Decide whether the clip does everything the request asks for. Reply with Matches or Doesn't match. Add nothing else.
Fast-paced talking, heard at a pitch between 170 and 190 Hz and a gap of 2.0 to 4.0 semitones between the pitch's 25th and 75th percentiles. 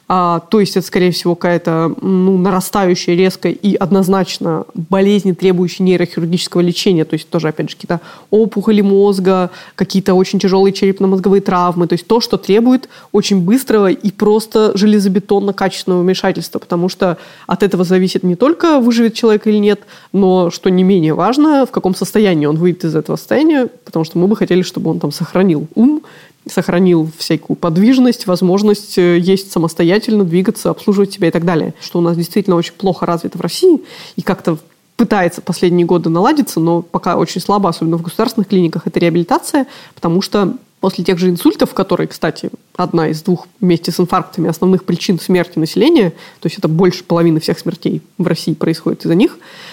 Matches